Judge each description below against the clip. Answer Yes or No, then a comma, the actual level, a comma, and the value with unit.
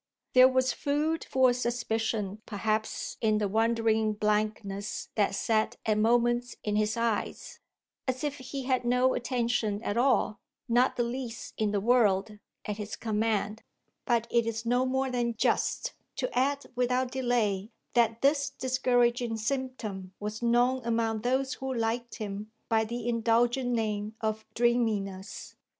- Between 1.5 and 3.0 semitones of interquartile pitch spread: Yes, narrow, 2.6 semitones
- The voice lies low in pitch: No, high, 235 Hz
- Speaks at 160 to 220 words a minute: No, average, 145 wpm